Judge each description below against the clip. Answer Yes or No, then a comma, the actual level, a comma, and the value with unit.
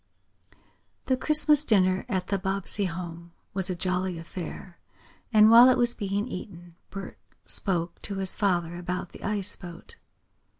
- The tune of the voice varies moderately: Yes, average, 3.0 semitones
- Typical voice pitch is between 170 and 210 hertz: Yes, high, 190 Hz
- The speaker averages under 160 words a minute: Yes, average, 145 wpm